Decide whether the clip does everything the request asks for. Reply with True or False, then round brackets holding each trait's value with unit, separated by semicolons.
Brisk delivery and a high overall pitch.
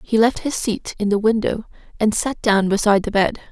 True (220 wpm; 215 Hz)